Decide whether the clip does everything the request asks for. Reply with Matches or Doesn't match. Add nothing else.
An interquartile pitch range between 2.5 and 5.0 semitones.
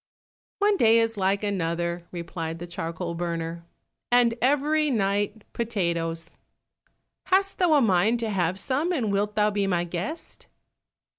Doesn't match